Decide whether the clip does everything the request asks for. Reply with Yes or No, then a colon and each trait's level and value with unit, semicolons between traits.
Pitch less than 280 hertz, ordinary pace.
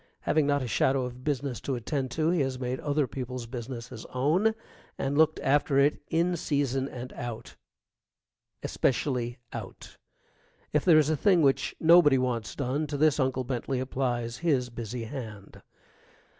Yes: low, 135 Hz; average, 160 wpm